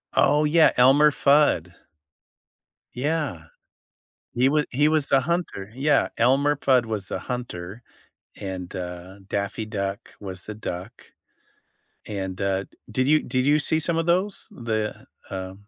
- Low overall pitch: Yes, low, 125 Hz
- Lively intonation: Yes, wide, 7.1 semitones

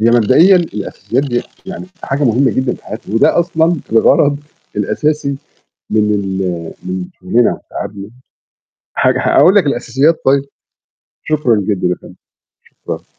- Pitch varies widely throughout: Yes, wide, 6.0 semitones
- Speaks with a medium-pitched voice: No, low, 130 Hz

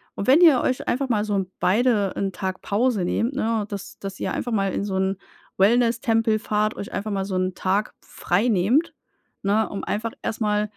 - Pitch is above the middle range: Yes, high, 210 Hz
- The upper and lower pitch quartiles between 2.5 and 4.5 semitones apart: Yes, average, 2.8 semitones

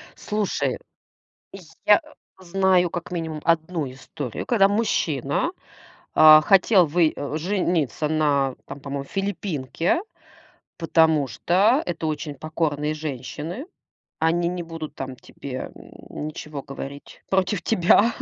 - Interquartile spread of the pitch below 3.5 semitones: No, average, 3.8 semitones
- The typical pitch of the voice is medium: Yes, medium, 160 Hz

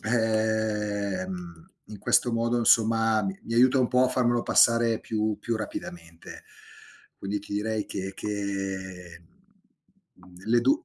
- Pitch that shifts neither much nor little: Yes, average, 3.1 semitones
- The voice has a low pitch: Yes, low, 110 Hz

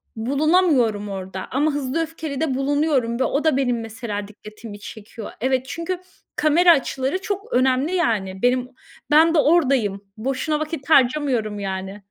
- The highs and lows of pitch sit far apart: Yes, wide, 5.9 semitones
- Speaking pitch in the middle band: No, very high, 260 Hz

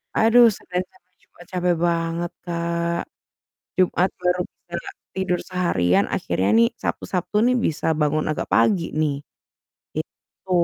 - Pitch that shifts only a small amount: Yes, narrow, 1.8 semitones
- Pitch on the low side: No, medium, 175 Hz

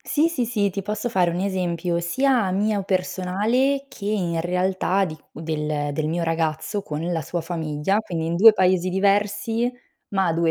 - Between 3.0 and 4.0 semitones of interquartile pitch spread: Yes, average, 3.7 semitones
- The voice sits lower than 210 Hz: Yes, medium, 185 Hz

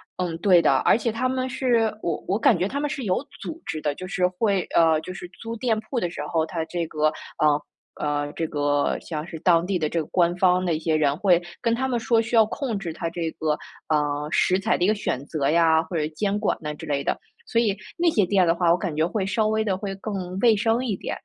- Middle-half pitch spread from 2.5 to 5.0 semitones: No, wide, 5.4 semitones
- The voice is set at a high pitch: No, medium, 180 Hz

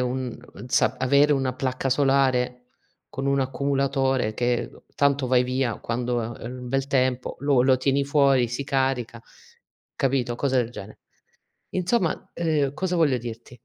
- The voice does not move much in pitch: Yes, narrow, 2.0 semitones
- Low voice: Yes, low, 130 Hz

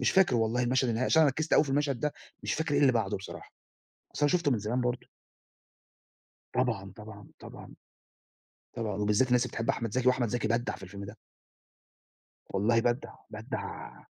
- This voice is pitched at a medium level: No, low, 120 Hz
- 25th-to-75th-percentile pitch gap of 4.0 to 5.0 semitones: No, average, 3.3 semitones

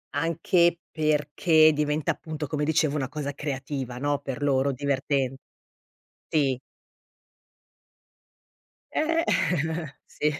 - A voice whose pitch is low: No, medium, 150 Hz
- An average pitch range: No, narrow, 2.1 semitones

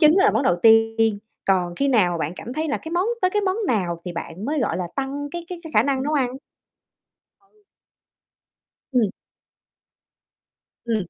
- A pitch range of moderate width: No, wide, 7.7 semitones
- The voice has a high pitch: Yes, very high, 250 Hz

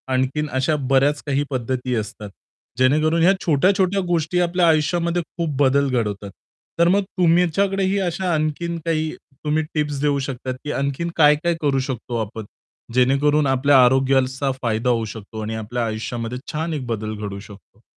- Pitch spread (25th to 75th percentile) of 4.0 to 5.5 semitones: Yes, average, 4.7 semitones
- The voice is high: No, medium, 140 Hz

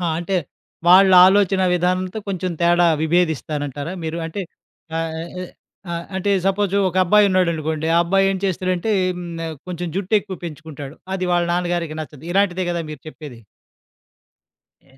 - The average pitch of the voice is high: No, medium, 175 Hz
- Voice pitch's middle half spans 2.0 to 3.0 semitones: Yes, average, 2.7 semitones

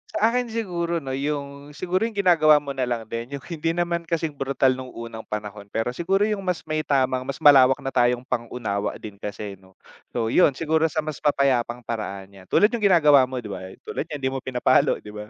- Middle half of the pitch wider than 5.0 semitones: Yes, wide, 5.4 semitones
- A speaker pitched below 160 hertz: Yes, low, 135 Hz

